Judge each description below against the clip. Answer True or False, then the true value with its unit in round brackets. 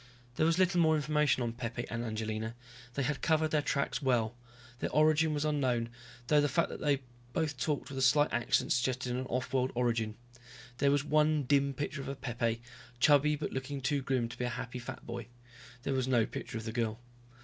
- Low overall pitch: True (130 Hz)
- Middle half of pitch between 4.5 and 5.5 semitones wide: False (3.7 semitones)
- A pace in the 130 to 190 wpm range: False (205 wpm)